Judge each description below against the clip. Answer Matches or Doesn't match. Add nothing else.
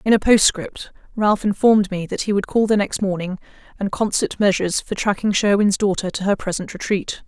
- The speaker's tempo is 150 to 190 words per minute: Doesn't match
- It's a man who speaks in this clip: Doesn't match